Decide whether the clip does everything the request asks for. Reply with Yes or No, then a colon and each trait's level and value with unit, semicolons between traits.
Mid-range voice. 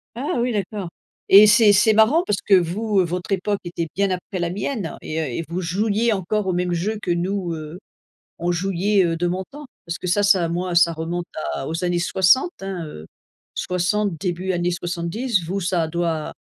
Yes: medium, 180 Hz